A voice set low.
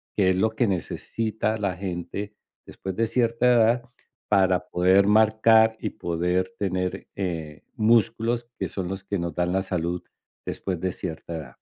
Yes: very low, 95 Hz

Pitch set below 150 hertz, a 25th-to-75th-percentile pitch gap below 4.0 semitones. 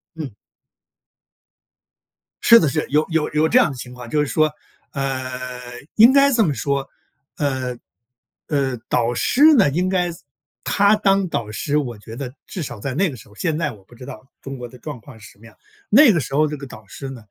No: medium, 140 Hz; average, 4.7 semitones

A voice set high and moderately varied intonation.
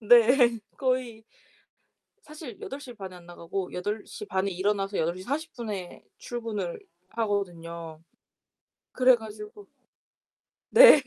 Yes: high, 210 Hz; average, 4.8 semitones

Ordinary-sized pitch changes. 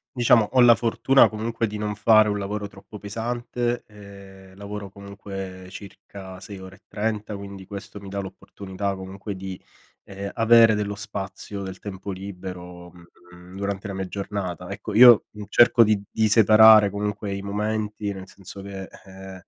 No: narrow, 1.8 semitones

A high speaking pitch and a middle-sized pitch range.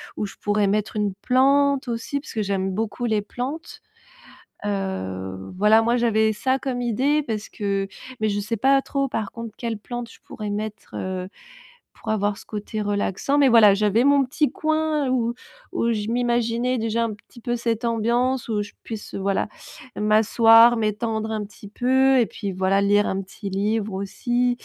Yes: high, 225 Hz; average, 3.0 semitones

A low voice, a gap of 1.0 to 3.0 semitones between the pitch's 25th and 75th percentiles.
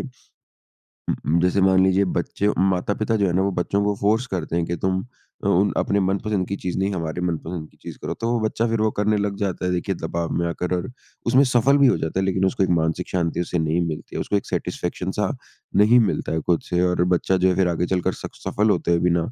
Yes: very low, 95 Hz; average, 2.7 semitones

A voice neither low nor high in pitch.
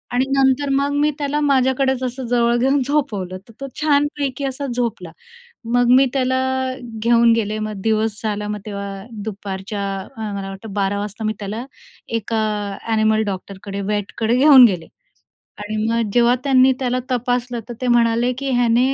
No: high, 235 Hz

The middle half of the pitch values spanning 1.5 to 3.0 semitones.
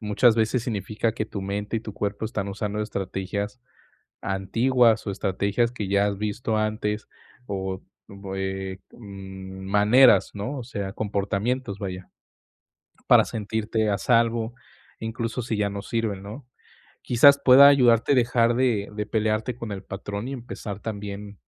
Yes: narrow, 2.6 semitones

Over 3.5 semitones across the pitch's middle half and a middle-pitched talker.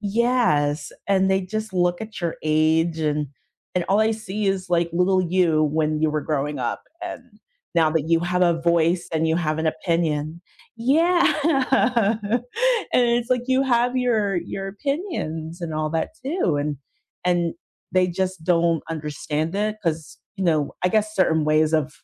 Yes: average, 4.7 semitones; medium, 175 Hz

